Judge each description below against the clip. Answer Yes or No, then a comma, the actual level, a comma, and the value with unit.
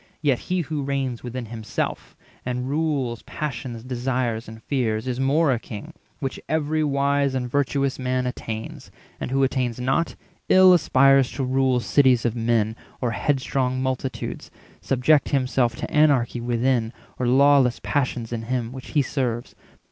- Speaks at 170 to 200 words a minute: No, average, 155 wpm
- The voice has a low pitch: Yes, low, 130 Hz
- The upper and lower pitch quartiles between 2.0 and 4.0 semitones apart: Yes, narrow, 2.5 semitones